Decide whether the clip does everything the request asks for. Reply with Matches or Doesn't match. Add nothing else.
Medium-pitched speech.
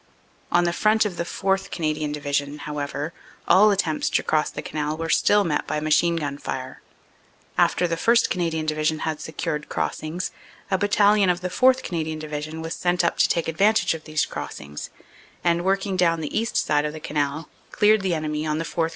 Matches